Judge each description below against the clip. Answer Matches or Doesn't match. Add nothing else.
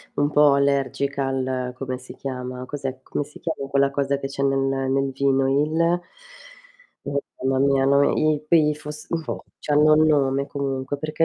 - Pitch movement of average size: Doesn't match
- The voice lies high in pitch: Doesn't match